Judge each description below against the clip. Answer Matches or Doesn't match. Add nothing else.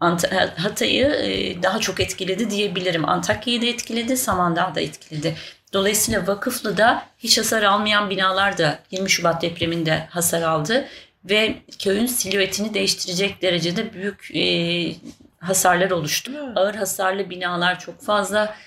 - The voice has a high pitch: Matches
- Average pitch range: Matches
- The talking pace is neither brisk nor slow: Matches